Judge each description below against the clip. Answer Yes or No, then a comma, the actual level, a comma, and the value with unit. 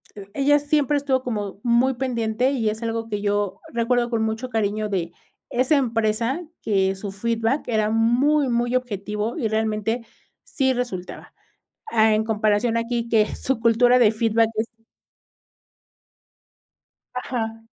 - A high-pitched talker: Yes, high, 230 Hz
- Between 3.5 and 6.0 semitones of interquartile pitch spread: No, narrow, 2.5 semitones